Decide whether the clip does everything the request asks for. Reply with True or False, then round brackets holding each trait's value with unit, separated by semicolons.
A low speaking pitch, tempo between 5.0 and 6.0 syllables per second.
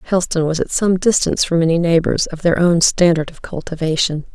False (170 Hz; 5.8 syllables/s)